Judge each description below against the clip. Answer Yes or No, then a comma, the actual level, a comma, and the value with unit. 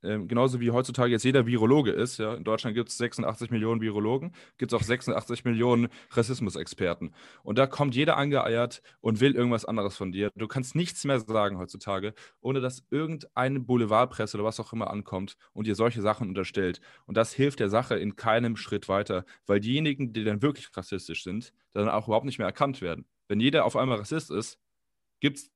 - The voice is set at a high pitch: No, low, 115 Hz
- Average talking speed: No, fast, 195 wpm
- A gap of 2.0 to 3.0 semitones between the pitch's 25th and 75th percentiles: No, average, 3.5 semitones